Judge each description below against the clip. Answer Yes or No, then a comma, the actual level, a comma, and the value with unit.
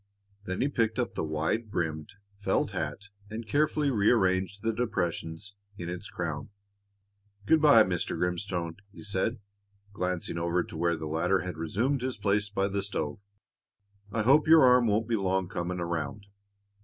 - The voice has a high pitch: No, low, 100 Hz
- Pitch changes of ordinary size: Yes, average, 4.6 semitones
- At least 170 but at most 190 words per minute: No, average, 160 wpm